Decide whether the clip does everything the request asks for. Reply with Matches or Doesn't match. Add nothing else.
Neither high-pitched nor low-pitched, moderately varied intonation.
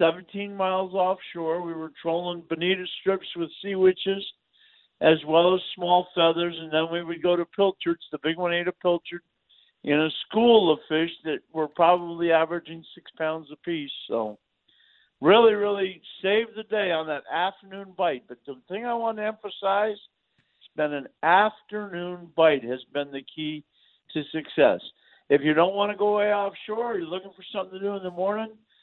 Matches